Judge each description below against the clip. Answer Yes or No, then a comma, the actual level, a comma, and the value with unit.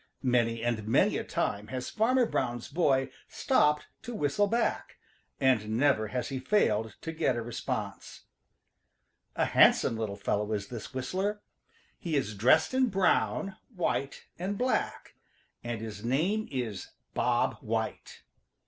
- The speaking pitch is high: No, low, 130 Hz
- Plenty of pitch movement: Yes, wide, 8.8 semitones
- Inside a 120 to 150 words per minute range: Yes, average, 140 wpm